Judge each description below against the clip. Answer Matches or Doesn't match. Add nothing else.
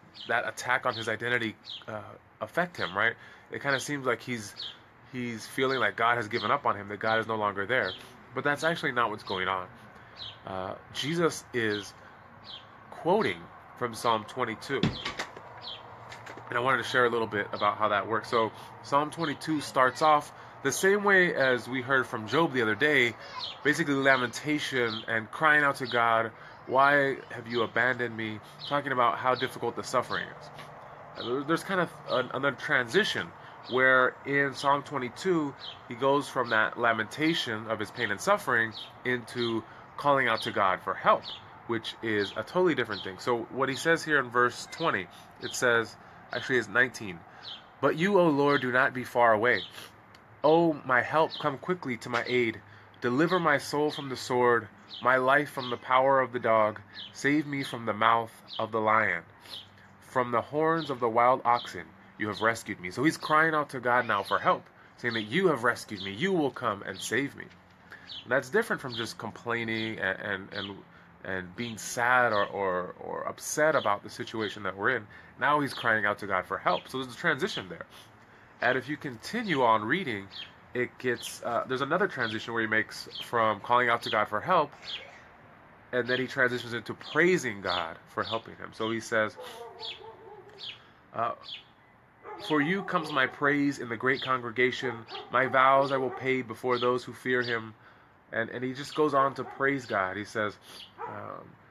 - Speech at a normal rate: Matches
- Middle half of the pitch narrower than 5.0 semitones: Matches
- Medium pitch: Doesn't match